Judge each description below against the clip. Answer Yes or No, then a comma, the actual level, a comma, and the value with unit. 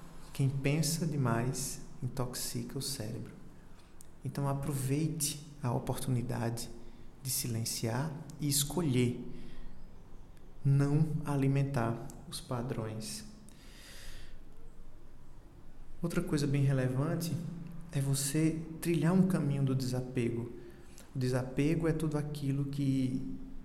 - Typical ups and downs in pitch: Yes, average, 3.8 semitones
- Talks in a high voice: No, low, 135 Hz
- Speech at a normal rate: No, slow, 90 wpm